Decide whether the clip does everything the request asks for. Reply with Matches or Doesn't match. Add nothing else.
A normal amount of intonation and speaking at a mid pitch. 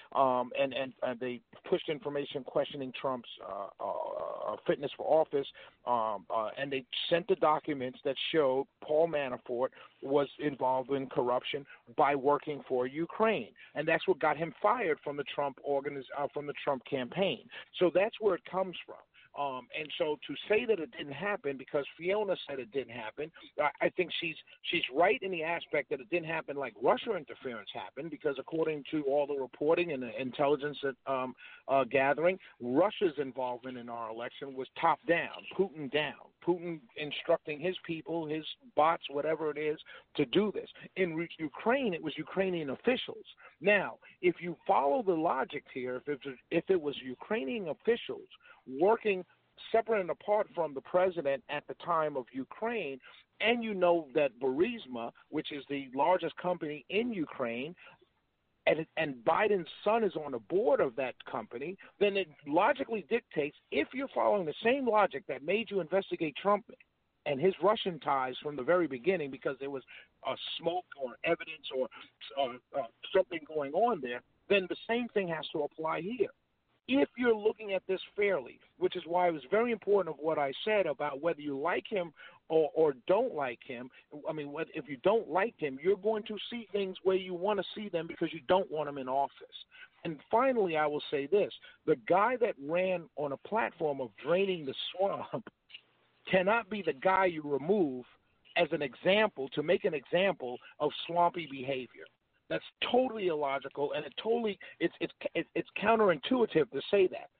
Doesn't match